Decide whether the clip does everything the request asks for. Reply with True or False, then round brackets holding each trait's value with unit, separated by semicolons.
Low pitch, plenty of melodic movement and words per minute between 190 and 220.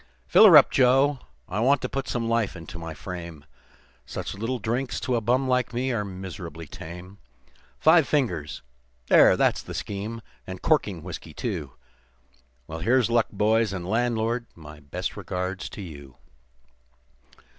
False (105 Hz; 6.0 semitones; 155 wpm)